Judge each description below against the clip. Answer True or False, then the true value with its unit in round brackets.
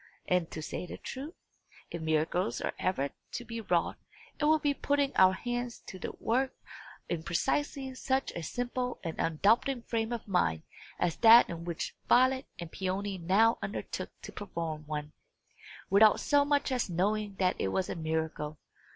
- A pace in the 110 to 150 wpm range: False (170 wpm)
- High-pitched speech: True (200 Hz)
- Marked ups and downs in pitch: True (6.7 semitones)